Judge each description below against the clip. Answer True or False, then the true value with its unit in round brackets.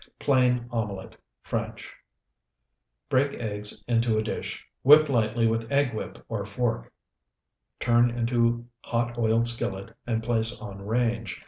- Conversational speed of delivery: False (125 wpm)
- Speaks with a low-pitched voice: True (115 Hz)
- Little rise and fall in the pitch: True (1.6 semitones)